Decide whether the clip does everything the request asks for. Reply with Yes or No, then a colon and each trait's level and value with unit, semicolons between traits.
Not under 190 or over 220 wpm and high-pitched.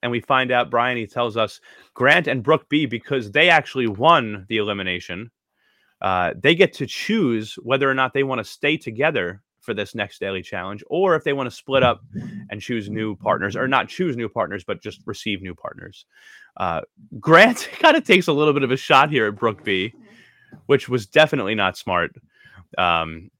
No: average, 200 wpm; low, 120 Hz